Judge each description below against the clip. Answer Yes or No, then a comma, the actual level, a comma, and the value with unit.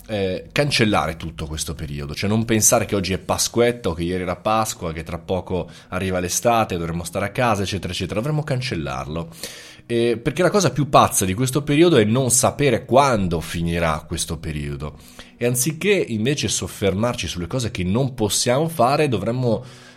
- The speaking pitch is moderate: No, low, 105 Hz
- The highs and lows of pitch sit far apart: Yes, wide, 5.8 semitones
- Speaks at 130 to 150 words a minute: No, fast, 170 wpm